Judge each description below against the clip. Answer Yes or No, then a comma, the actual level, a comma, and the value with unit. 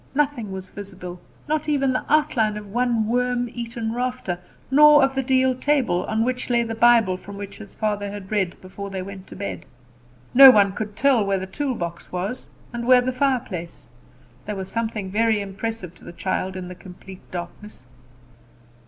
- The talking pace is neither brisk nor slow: Yes, average, 180 wpm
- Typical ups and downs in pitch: Yes, average, 4.6 semitones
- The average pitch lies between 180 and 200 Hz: No, high, 220 Hz